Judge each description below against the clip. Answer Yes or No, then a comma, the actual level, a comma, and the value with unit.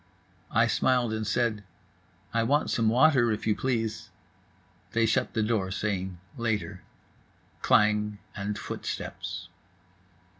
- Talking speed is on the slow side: Yes, slow, 115 wpm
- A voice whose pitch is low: Yes, low, 110 Hz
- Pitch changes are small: Yes, narrow, 2.1 semitones